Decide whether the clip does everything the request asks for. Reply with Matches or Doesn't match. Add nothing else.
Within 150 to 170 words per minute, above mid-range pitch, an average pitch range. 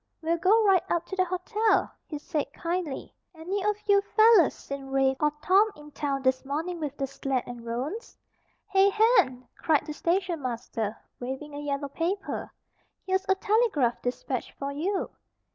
Doesn't match